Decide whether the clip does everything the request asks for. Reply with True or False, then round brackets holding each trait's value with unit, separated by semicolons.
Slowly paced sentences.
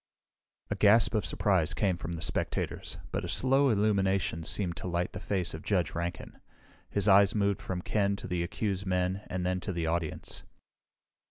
False (180 wpm)